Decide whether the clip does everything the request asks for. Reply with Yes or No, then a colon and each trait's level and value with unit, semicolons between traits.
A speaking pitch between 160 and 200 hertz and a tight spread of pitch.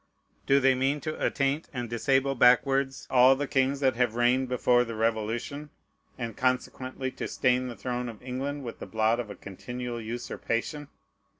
No: low, 125 Hz; narrow, 2.3 semitones